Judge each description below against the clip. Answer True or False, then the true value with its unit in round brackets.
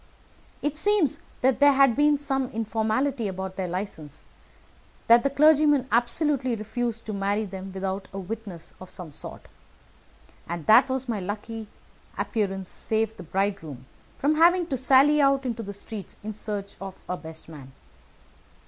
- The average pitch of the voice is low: False (220 Hz)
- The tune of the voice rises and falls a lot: True (5.8 semitones)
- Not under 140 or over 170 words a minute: True (150 wpm)